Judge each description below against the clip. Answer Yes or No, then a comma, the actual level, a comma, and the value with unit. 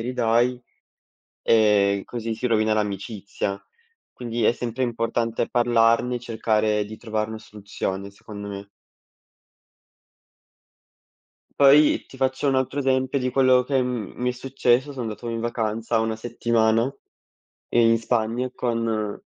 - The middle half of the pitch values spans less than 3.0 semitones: Yes, narrow, 2.4 semitones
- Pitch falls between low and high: No, low, 115 Hz